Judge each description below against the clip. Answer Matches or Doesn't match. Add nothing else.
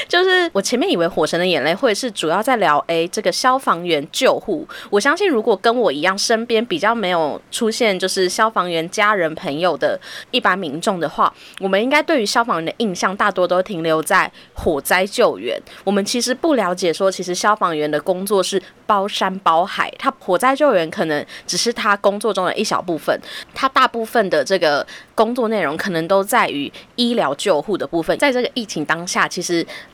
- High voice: Matches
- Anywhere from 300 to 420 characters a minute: Matches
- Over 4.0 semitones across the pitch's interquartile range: Matches